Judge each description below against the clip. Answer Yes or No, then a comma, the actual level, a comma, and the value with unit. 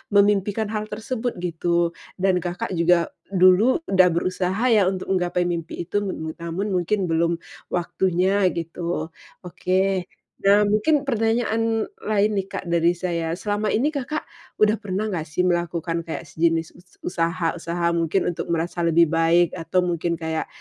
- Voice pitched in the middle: Yes, medium, 180 Hz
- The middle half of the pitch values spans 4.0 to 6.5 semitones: No, average, 3.3 semitones